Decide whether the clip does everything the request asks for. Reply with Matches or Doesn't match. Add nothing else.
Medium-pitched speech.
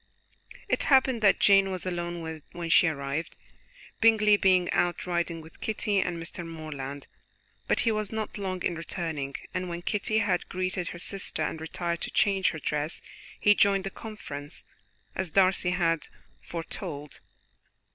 Matches